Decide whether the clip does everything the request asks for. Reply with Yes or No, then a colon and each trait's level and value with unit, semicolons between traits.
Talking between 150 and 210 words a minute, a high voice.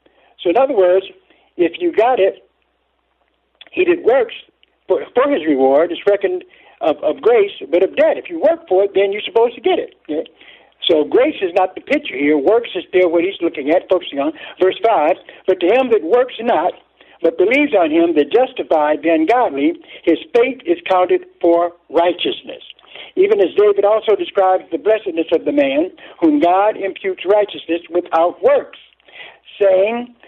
Yes: average, 180 wpm; high, 210 Hz